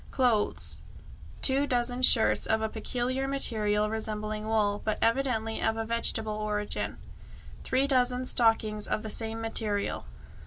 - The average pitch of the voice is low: No, high, 225 Hz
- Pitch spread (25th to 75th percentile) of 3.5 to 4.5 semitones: No, narrow, 2.6 semitones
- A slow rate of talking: Yes, slow, 130 wpm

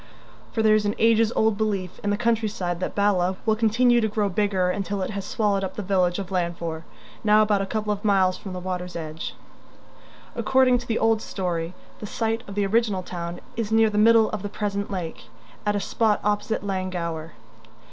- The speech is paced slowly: No, fast, 205 wpm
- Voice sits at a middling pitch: No, high, 205 Hz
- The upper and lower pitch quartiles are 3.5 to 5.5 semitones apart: No, average, 3.0 semitones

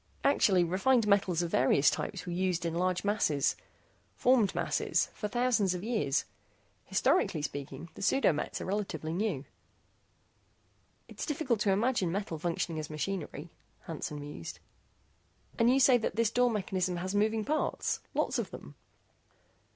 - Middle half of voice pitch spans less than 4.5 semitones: No, average, 5.0 semitones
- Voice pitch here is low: No, high, 190 Hz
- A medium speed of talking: Yes, average, 145 wpm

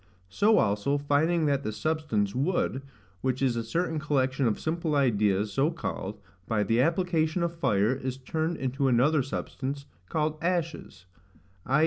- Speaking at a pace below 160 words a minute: Yes, average, 150 wpm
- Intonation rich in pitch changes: No, average, 4.6 semitones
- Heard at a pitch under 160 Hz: Yes, medium, 140 Hz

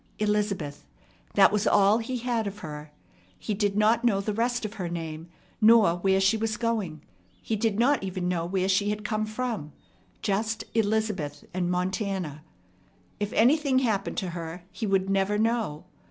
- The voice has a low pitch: No, high, 205 Hz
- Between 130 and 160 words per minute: No, average, 170 wpm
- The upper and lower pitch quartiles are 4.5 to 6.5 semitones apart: No, average, 3.4 semitones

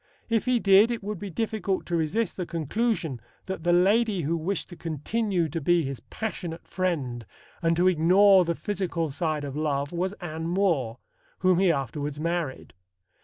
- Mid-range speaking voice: Yes, medium, 175 Hz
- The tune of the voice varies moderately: Yes, average, 3.9 semitones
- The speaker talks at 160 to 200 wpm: Yes, average, 170 wpm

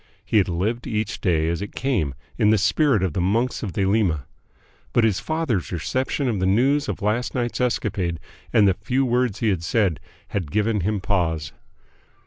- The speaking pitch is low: Yes, low, 105 Hz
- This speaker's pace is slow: No, average, 185 wpm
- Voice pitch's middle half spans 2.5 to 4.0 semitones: No, average, 4.8 semitones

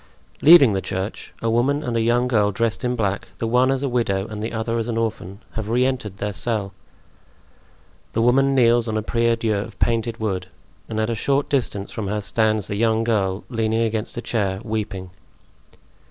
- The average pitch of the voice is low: Yes, low, 115 Hz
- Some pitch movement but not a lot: No, narrow, 2.3 semitones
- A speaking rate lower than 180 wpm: No, average, 200 wpm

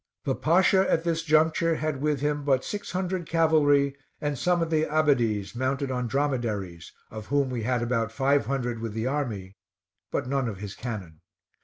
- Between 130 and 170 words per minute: No, average, 180 wpm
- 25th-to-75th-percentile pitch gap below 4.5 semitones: No, average, 4.9 semitones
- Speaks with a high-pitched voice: No, medium, 140 Hz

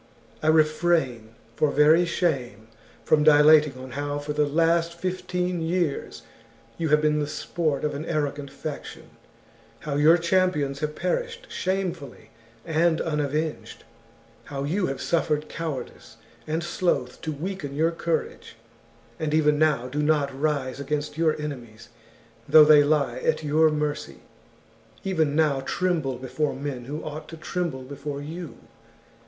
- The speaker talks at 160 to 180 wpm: No, average, 140 wpm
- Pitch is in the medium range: Yes, medium, 150 Hz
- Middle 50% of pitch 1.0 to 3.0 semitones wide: Yes, narrow, 2.5 semitones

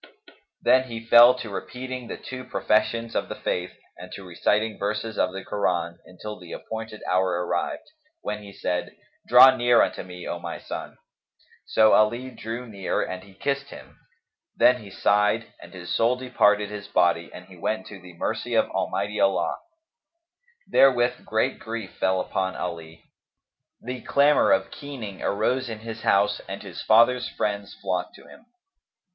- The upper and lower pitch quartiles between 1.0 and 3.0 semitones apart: No, average, 4.7 semitones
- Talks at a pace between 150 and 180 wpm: Yes, average, 165 wpm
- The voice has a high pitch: No, low, 105 Hz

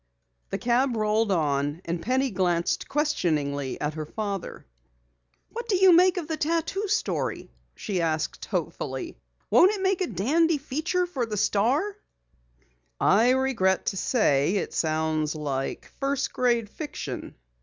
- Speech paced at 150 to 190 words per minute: No, average, 140 wpm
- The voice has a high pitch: Yes, high, 225 Hz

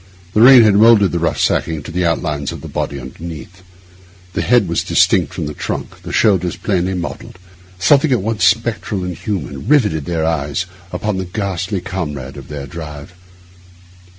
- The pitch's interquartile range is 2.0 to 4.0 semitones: No, average, 4.8 semitones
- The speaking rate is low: No, average, 175 wpm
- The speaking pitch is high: No, very low, 90 Hz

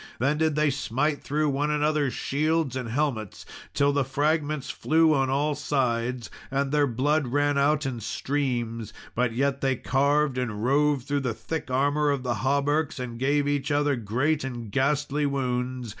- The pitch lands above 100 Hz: Yes, medium, 140 Hz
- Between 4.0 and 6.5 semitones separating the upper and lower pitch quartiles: No, narrow, 2.6 semitones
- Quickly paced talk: No, average, 170 wpm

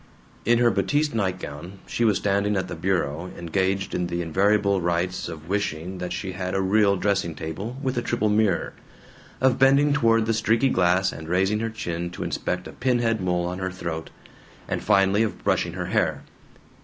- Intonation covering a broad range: No, average, 3.9 semitones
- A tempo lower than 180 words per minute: No, average, 190 wpm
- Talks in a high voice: No, very low, 95 Hz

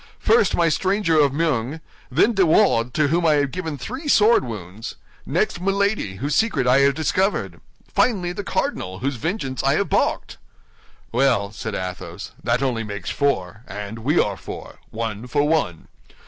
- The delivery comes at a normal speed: Yes, average, 160 wpm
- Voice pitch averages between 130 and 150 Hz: Yes, medium, 140 Hz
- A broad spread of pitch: Yes, wide, 7.8 semitones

